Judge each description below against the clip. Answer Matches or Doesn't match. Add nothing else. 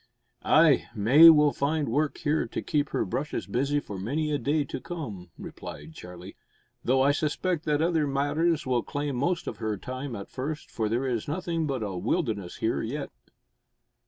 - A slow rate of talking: Doesn't match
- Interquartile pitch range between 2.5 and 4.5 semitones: Doesn't match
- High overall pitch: Doesn't match